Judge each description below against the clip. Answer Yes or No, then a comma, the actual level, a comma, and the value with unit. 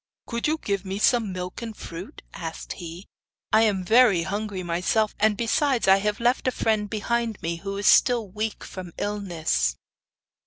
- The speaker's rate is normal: Yes, average, 170 wpm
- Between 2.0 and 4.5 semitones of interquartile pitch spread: Yes, average, 3.6 semitones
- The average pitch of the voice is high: Yes, high, 205 Hz